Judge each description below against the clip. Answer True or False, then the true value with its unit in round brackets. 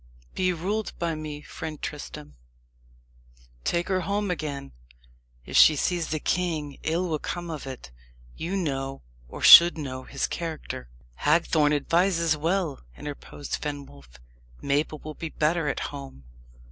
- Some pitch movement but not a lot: True (3.3 semitones)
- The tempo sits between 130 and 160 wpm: True (135 wpm)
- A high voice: False (155 Hz)